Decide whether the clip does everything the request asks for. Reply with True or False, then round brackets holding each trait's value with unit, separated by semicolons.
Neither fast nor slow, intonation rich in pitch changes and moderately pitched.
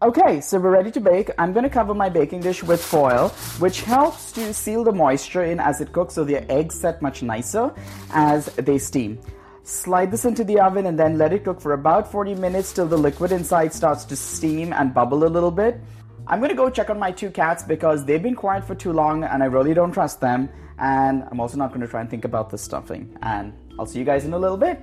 False (240 wpm; 6.0 semitones; 160 Hz)